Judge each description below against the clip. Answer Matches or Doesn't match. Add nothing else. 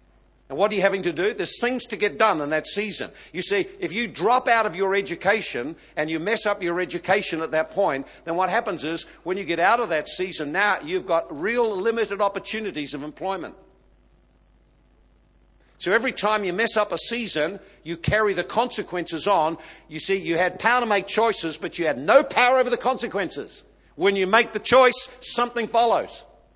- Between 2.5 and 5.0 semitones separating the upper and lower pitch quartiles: Doesn't match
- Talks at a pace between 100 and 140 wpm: Doesn't match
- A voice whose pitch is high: Matches